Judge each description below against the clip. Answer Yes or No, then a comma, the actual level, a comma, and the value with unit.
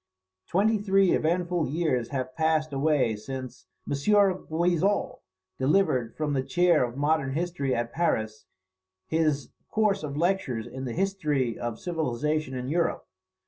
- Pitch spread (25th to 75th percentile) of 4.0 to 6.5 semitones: Yes, average, 5.2 semitones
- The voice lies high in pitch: No, medium, 155 Hz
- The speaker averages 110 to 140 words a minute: Yes, slow, 135 wpm